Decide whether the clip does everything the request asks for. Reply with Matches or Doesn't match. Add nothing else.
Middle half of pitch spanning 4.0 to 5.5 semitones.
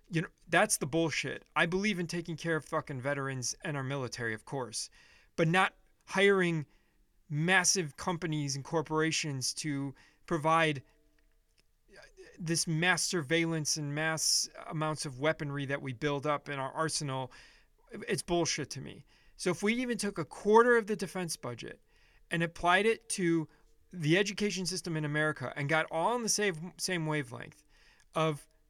Doesn't match